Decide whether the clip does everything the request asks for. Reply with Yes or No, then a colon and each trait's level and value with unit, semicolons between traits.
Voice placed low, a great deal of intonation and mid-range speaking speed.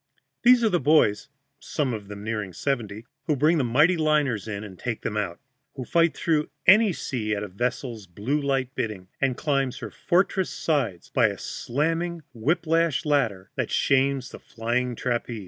Yes: low, 130 Hz; wide, 6.1 semitones; average, 180 wpm